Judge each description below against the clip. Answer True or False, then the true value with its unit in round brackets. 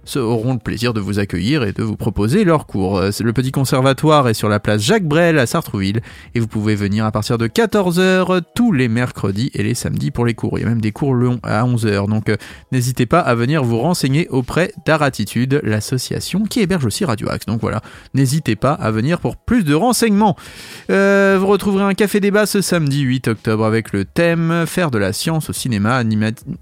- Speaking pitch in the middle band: False (130 Hz)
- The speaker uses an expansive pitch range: True (7.4 semitones)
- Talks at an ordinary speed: True (210 wpm)